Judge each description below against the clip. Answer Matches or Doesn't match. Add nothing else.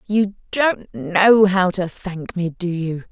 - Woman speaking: Matches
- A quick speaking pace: Doesn't match